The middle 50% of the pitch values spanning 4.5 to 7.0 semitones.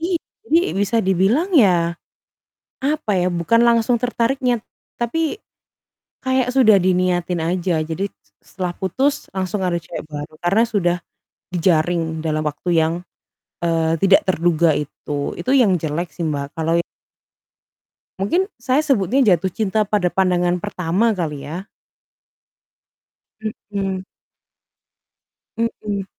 Yes: wide, 5.4 semitones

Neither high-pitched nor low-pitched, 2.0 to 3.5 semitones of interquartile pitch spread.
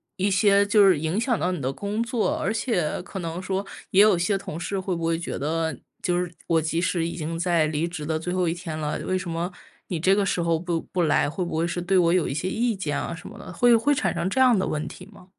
Yes: medium, 175 Hz; average, 3.1 semitones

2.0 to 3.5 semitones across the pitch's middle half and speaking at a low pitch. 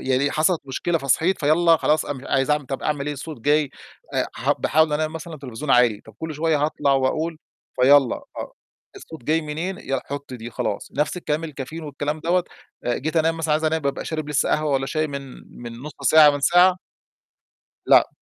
No: narrow, 2.6 semitones; medium, 150 Hz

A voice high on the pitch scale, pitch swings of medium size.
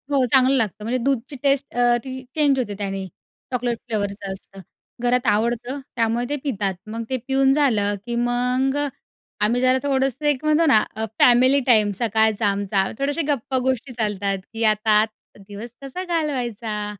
Yes: high, 245 Hz; average, 4.0 semitones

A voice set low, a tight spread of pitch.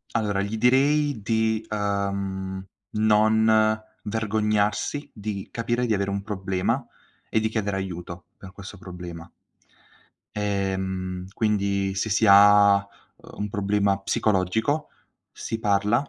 Yes: low, 105 Hz; narrow, 2.1 semitones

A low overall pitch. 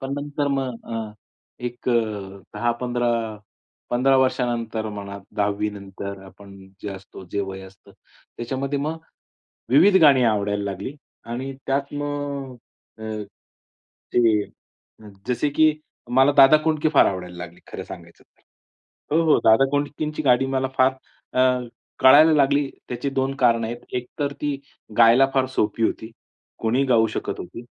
Yes: low, 125 Hz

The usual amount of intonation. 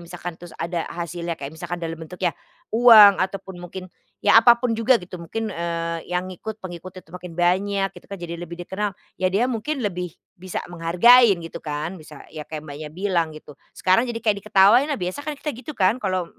Yes: average, 3.9 semitones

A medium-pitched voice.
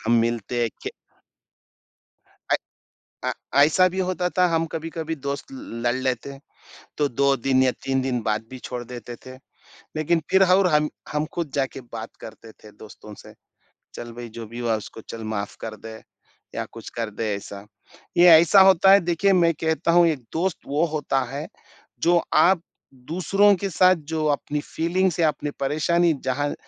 Yes: medium, 145 Hz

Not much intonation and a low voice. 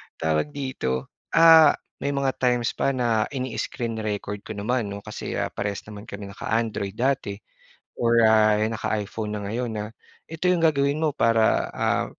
No: average, 4.1 semitones; low, 115 Hz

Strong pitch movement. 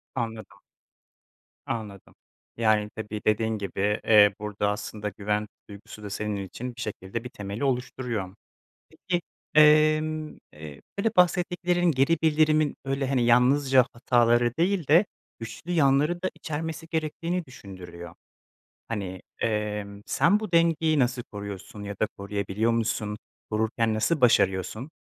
Yes: wide, 6.6 semitones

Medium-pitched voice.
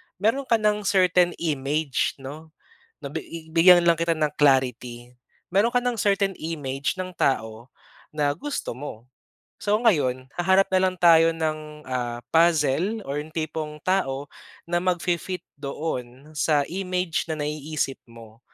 Yes: medium, 160 Hz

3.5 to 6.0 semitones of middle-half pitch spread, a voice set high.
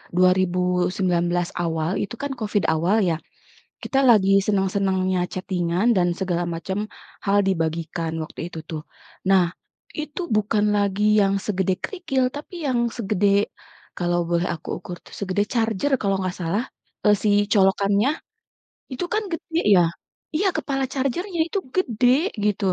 Yes: average, 4.0 semitones; high, 195 Hz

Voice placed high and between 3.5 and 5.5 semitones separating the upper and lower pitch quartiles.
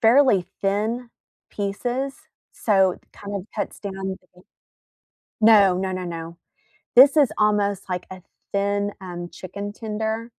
No: high, 200 Hz; average, 2.8 semitones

